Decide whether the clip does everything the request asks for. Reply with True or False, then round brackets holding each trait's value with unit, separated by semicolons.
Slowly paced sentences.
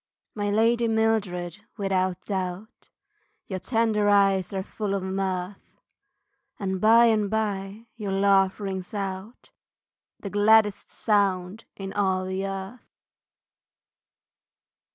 True (110 wpm)